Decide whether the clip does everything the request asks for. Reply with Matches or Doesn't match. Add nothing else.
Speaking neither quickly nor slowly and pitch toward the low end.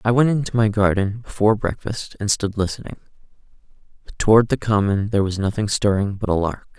Matches